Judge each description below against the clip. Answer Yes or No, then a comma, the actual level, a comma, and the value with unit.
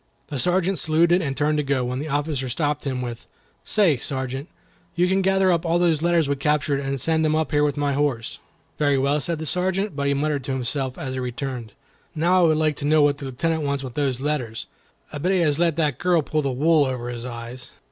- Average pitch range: Yes, average, 3.4 semitones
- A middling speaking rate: No, fast, 240 wpm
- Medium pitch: Yes, medium, 145 Hz